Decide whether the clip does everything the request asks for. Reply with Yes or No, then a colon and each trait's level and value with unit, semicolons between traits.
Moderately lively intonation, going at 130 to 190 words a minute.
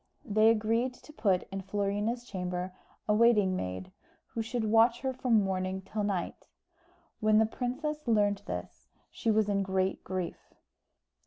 Yes: average, 3.3 semitones; average, 150 wpm